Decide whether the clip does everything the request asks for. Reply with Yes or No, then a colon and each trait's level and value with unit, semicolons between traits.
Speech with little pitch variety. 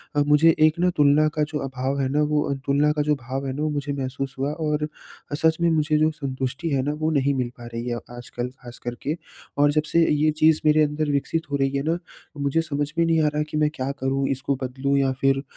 Yes: narrow, 2.1 semitones